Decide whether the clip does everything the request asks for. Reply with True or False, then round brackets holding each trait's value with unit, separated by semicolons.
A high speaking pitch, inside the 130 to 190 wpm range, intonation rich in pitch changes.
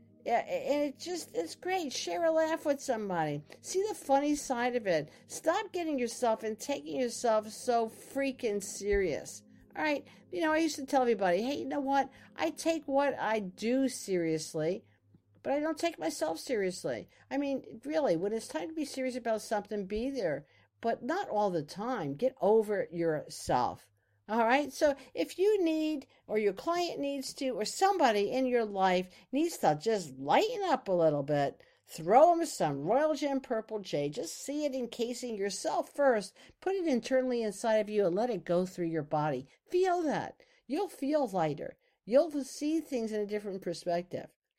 True (250 Hz; 180 wpm; 6.4 semitones)